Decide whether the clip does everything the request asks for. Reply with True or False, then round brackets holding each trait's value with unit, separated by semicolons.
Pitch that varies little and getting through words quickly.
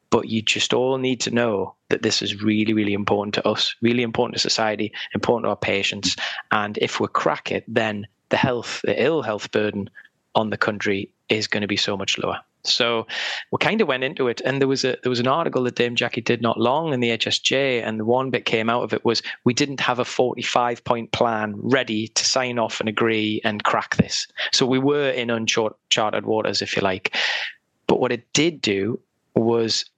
True (2.3 semitones; 220 wpm)